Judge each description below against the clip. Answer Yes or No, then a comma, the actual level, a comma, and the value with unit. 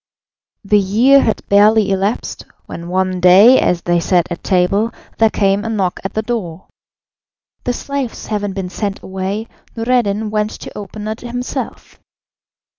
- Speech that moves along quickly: No, average, 150 wpm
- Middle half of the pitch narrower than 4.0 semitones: Yes, average, 2.9 semitones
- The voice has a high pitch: Yes, high, 205 Hz